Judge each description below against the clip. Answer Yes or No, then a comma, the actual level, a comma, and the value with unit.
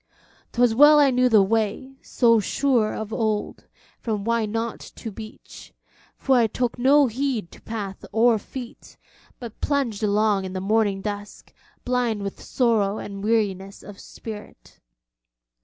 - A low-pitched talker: No, high, 220 Hz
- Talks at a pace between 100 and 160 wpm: Yes, average, 145 wpm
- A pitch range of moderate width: Yes, average, 3.1 semitones